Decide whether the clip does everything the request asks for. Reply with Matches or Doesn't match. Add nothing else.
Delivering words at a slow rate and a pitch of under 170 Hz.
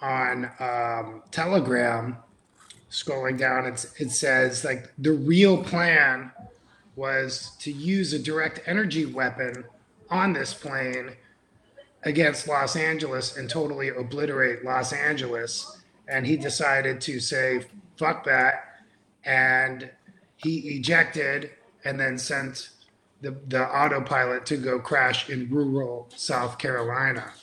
Matches